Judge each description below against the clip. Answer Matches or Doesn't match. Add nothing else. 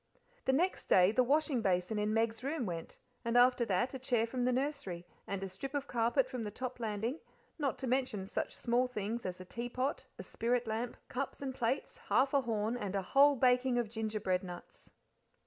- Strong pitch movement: Doesn't match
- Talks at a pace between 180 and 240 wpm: Matches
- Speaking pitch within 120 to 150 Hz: Doesn't match